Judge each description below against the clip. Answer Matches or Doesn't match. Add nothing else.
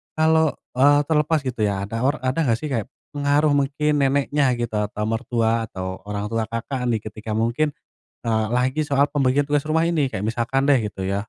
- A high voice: Doesn't match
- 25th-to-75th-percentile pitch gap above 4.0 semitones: Matches